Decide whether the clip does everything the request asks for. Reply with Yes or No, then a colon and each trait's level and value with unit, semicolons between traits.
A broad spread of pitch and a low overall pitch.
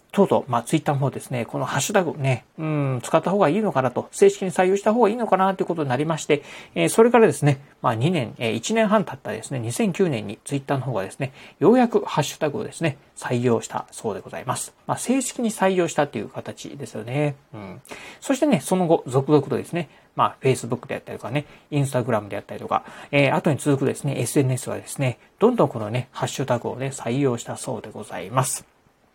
No: wide, 6.4 semitones; medium, 145 Hz